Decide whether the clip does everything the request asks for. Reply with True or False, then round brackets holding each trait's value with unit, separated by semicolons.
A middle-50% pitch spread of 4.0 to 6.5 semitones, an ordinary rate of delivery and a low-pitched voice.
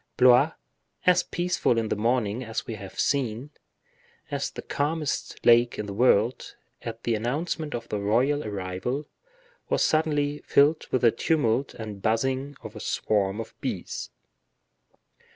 True (4.7 semitones; 145 wpm; 120 Hz)